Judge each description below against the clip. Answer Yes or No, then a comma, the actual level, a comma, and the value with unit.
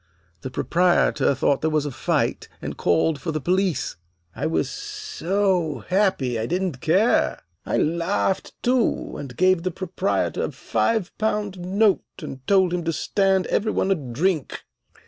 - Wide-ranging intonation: No, average, 4.3 semitones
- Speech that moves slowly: No, average, 155 wpm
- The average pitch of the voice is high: No, medium, 180 Hz